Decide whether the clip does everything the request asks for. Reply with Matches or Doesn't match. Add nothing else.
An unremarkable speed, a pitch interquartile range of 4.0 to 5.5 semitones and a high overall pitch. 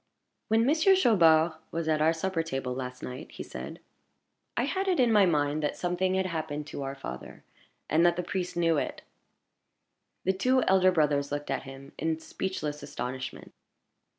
Doesn't match